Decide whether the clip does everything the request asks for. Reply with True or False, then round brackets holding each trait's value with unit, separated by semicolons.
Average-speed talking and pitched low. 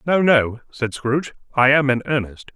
True (190 wpm; 130 Hz)